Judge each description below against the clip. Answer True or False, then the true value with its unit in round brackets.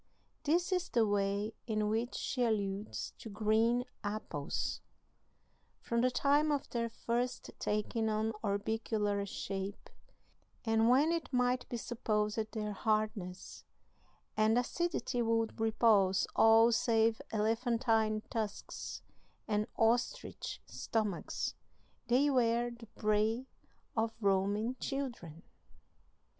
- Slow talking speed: True (105 wpm)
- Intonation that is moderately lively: False (2.3 semitones)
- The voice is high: True (225 Hz)